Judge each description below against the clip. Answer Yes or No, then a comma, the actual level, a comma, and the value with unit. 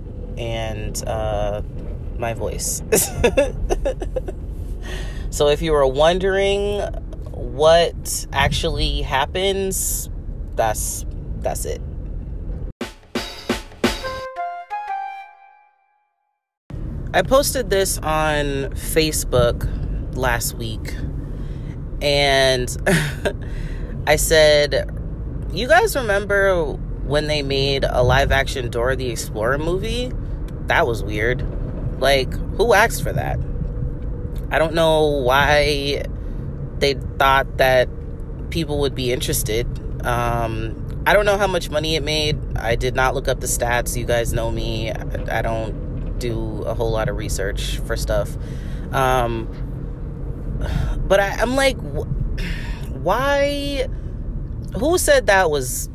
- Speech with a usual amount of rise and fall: No, wide, 6.1 semitones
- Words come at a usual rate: No, slow, 105 wpm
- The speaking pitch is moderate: No, low, 130 Hz